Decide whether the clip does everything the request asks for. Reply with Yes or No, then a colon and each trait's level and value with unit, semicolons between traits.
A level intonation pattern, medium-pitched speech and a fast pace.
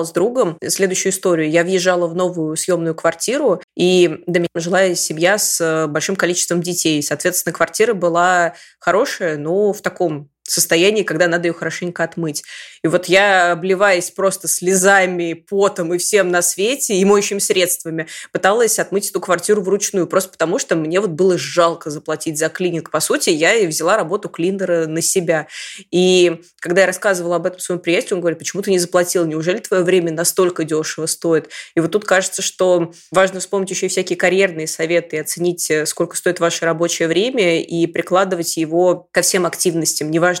Yes: narrow, 2.0 semitones; medium, 175 Hz; fast, 170 wpm